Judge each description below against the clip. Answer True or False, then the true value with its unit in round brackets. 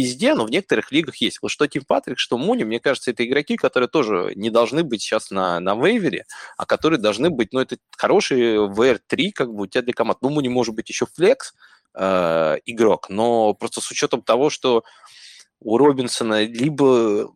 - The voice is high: False (120 Hz)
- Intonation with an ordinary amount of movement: True (3.3 semitones)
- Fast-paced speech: True (195 wpm)